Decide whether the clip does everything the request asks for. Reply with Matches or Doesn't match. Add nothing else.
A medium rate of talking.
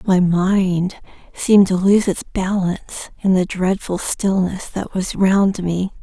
Matches